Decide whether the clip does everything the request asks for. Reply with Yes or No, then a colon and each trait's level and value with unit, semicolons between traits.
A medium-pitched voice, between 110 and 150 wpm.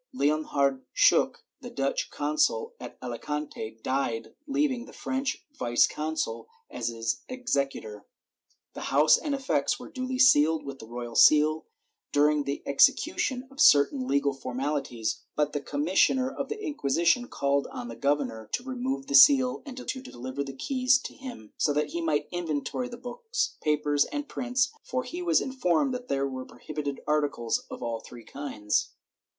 No: medium, 150 Hz; average, 160 wpm